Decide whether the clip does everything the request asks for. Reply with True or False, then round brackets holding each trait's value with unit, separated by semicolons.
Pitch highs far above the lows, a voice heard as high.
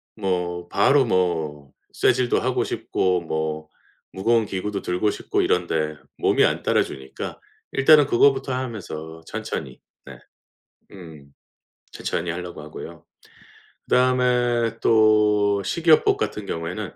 False (6.5 semitones; 95 Hz)